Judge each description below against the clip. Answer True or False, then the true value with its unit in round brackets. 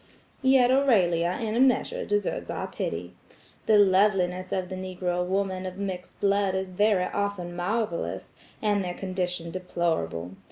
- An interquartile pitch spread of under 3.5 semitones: True (2.4 semitones)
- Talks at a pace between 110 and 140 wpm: True (135 wpm)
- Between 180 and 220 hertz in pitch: True (185 Hz)